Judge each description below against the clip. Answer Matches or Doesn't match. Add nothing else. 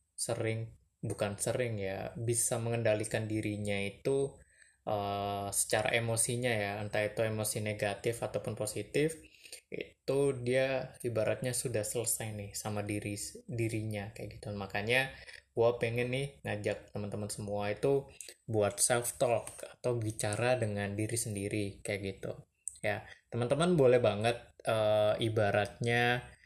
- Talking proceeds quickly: Doesn't match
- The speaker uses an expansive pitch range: Doesn't match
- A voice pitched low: Matches